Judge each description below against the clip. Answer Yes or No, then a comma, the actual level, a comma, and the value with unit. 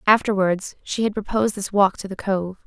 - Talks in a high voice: Yes, high, 200 Hz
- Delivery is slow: No, fast, 205 wpm